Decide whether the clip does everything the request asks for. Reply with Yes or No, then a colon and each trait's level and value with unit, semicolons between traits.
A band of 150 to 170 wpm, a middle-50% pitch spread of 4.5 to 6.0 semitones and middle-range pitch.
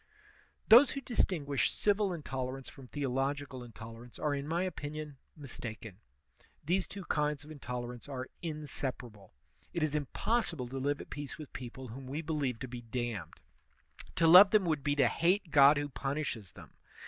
No: average, 160 wpm; average, 3.8 semitones; medium, 145 Hz